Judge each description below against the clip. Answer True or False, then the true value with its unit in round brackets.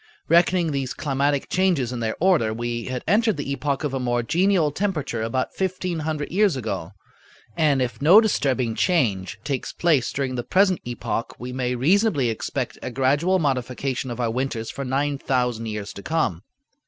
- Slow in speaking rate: False (175 wpm)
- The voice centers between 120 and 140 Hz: True (135 Hz)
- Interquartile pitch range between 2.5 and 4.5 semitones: False (5.3 semitones)